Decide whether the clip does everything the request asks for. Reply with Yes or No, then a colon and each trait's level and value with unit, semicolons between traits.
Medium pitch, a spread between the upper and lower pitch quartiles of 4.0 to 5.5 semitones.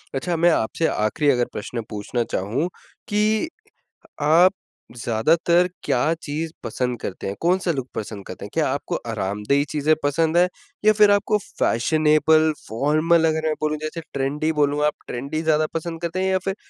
Yes: medium, 155 Hz; average, 4.8 semitones